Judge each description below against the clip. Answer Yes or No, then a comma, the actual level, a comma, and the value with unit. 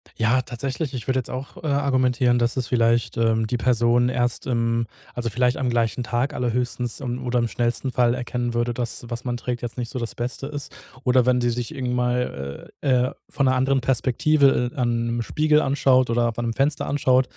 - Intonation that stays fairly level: Yes, narrow, 1.6 semitones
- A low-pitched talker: Yes, low, 125 Hz